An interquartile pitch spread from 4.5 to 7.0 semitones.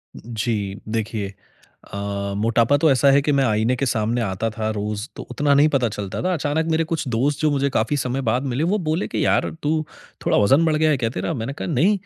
Yes: average, 4.9 semitones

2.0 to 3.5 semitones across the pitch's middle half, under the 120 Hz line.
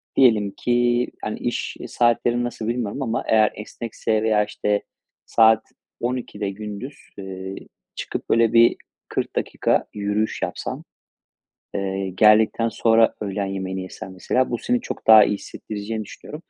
Yes: narrow, 2.6 semitones; low, 110 Hz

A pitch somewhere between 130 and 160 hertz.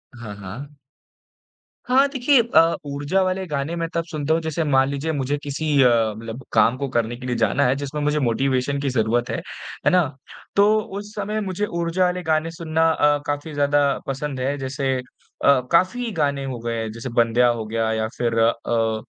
Yes: medium, 140 Hz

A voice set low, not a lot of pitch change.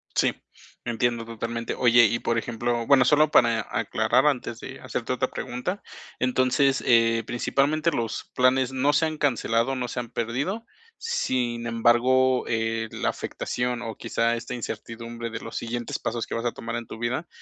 Yes: low, 120 Hz; narrow, 2.0 semitones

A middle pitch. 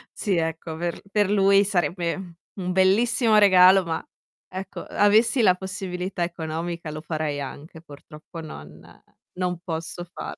Yes: medium, 180 Hz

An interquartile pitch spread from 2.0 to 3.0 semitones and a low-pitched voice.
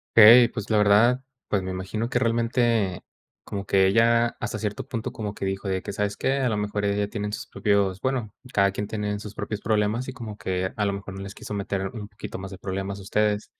Yes: narrow, 2.4 semitones; low, 105 Hz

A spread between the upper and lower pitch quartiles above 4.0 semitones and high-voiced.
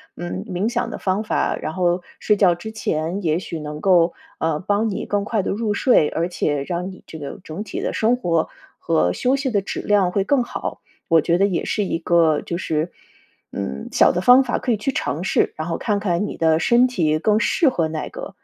No: average, 4.5 semitones; medium, 180 Hz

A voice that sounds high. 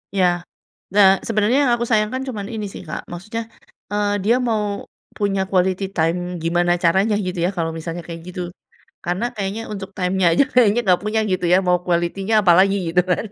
Yes: high, 195 Hz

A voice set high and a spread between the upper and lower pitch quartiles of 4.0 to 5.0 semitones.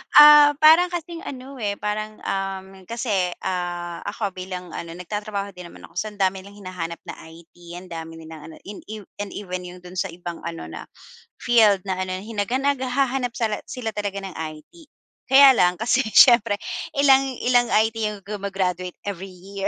Yes: high, 200 Hz; average, 4.7 semitones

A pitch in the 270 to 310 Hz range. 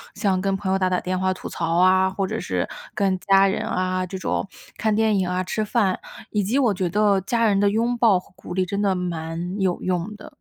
No: high, 190 Hz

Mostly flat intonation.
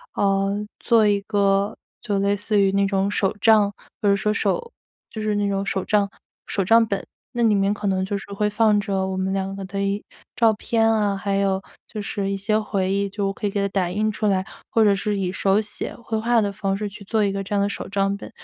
Yes: narrow, 1.3 semitones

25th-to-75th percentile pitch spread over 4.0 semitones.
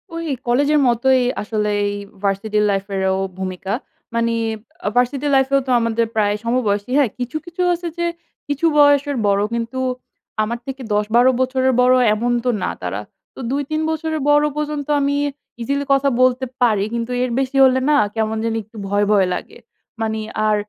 Yes: average, 4.6 semitones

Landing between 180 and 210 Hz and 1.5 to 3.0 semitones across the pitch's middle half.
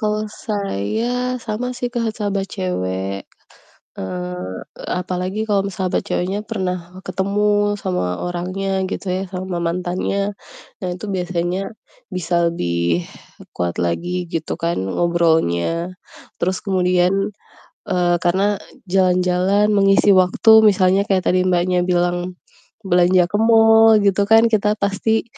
Yes: medium, 185 Hz; narrow, 2.5 semitones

